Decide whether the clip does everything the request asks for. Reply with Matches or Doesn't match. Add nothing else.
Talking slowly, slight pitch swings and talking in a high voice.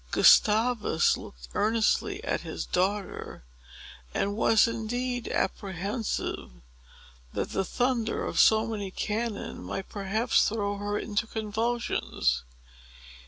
Matches